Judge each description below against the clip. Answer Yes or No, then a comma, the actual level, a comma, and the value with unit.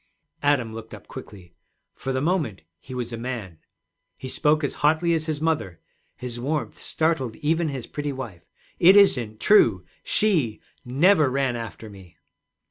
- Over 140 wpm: Yes, average, 155 wpm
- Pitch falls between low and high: No, low, 130 Hz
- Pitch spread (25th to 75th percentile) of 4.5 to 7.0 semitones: Yes, wide, 5.6 semitones